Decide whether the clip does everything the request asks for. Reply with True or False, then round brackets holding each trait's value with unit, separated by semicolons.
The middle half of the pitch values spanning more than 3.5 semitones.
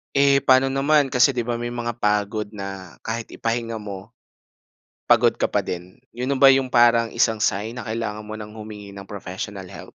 False (3.0 semitones)